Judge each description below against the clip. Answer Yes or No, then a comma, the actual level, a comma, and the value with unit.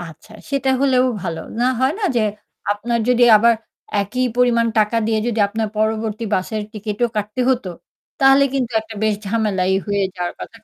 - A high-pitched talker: Yes, high, 225 Hz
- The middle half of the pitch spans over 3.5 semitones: No, average, 2.9 semitones